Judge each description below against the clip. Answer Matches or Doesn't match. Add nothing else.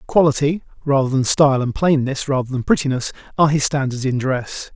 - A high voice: Doesn't match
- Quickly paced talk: Doesn't match